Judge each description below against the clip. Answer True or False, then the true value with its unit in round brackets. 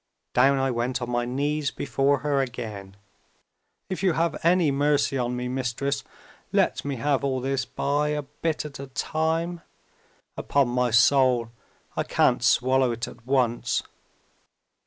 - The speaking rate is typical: True (150 wpm)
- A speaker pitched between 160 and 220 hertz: False (135 Hz)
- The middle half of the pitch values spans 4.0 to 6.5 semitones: False (2.8 semitones)